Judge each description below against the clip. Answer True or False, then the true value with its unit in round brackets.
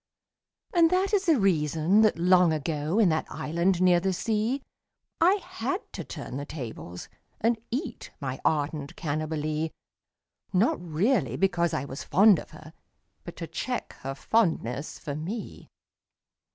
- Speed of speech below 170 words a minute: True (150 wpm)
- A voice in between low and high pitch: True (170 Hz)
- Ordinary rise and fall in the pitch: False (6.3 semitones)